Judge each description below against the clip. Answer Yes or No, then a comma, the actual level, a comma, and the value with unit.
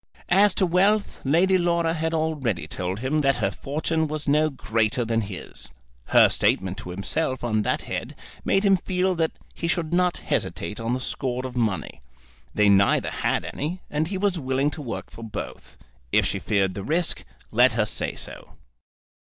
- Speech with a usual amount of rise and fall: No, wide, 7.1 semitones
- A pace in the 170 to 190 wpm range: Yes, average, 180 wpm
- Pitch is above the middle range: No, medium, 145 Hz